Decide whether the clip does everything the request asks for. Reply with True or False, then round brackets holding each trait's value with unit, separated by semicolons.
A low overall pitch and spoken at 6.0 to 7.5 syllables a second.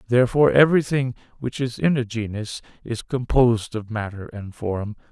False (120 Hz; 5.4 syllables/s)